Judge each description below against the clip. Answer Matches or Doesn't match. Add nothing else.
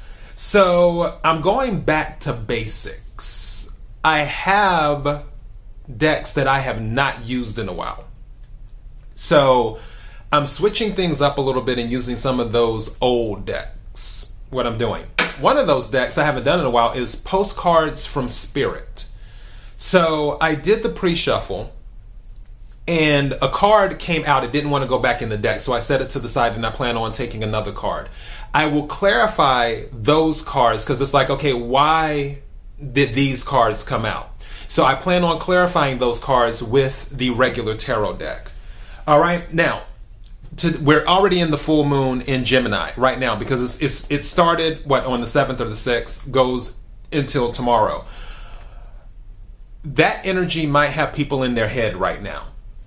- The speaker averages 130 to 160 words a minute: Doesn't match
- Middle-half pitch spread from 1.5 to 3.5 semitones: Doesn't match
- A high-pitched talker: Doesn't match